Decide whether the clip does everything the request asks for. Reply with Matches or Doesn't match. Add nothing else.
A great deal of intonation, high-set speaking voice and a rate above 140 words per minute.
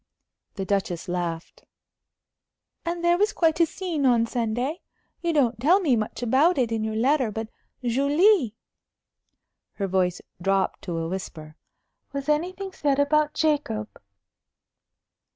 Doesn't match